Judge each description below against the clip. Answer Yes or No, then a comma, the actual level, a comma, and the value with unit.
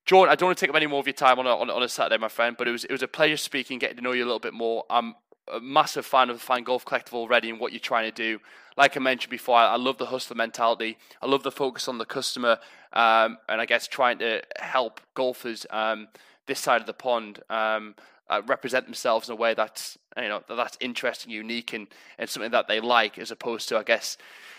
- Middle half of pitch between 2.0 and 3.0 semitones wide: Yes, narrow, 2.5 semitones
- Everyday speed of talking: No, fast, 260 wpm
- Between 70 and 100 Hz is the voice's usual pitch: No, low, 120 Hz